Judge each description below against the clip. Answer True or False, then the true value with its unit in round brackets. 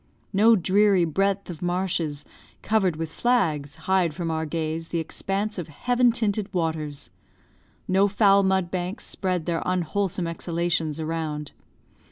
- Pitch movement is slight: False (3.5 semitones)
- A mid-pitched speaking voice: True (175 Hz)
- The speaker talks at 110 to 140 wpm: True (135 wpm)